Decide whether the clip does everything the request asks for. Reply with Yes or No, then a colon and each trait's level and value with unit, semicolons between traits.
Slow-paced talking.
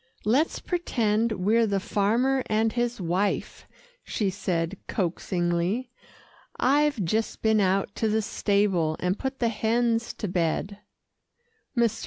Yes: slow, 125 wpm